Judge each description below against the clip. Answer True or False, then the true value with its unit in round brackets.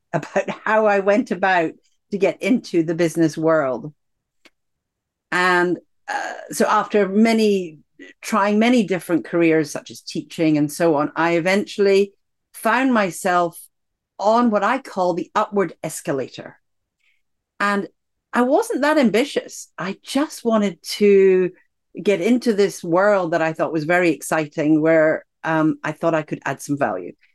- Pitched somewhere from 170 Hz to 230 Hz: True (185 Hz)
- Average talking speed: True (145 wpm)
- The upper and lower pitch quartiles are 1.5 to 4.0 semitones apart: False (4.7 semitones)